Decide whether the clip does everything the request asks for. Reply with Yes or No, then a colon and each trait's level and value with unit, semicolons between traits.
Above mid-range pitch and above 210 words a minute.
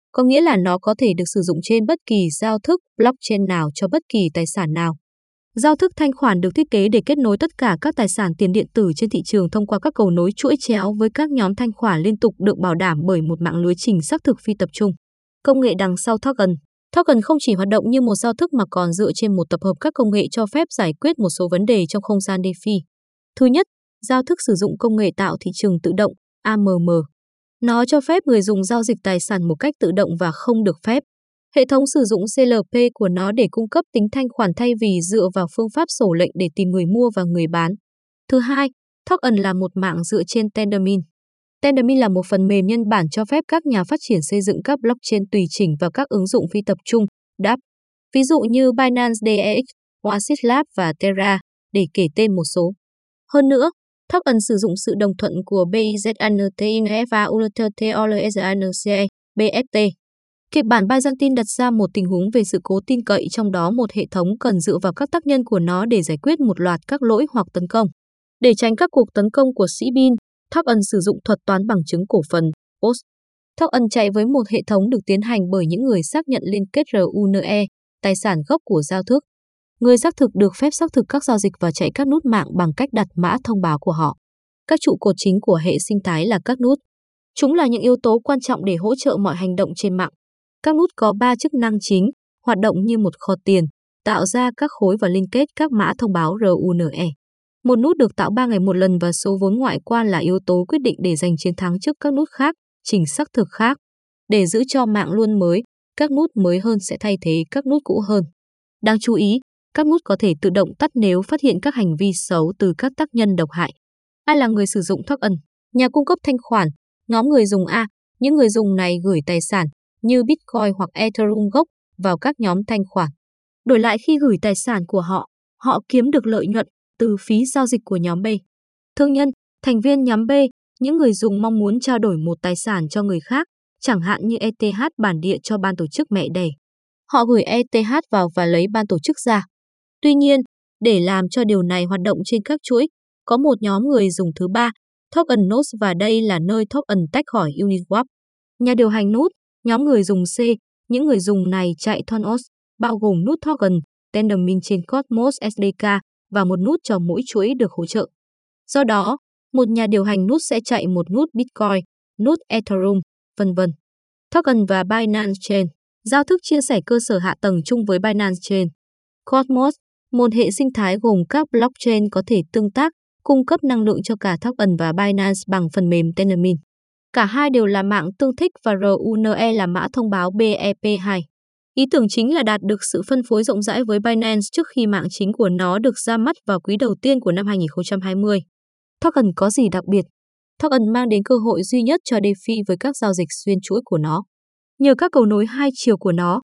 Yes: high, 215 Hz; average, 225 wpm